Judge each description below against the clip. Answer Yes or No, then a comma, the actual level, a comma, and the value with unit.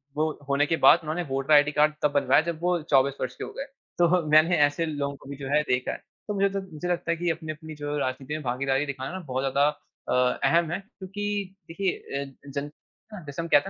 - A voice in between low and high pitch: Yes, medium, 155 Hz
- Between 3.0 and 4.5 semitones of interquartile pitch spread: Yes, average, 3.8 semitones